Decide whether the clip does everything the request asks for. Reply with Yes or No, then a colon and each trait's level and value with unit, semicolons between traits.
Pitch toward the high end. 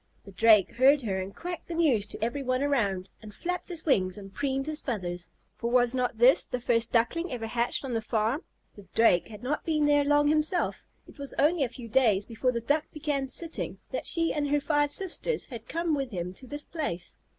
Yes: very high, 255 Hz